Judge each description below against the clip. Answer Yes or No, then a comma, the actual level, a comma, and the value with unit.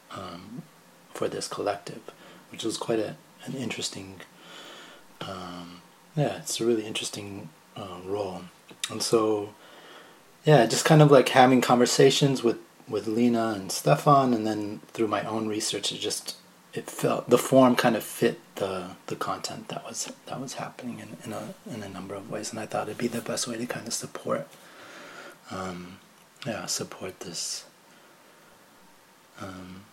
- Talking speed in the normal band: Yes, average, 160 wpm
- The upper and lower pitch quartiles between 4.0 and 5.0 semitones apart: Yes, average, 4.5 semitones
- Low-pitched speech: Yes, low, 110 Hz